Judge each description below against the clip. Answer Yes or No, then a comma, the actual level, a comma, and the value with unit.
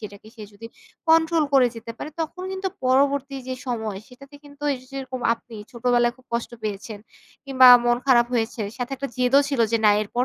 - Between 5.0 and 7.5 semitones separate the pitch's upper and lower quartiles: No, average, 3.0 semitones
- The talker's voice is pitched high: Yes, very high, 255 Hz